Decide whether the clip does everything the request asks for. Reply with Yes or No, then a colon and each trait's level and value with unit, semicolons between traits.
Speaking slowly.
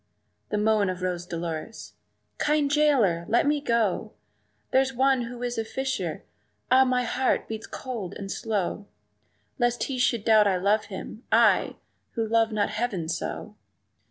No: average, 155 wpm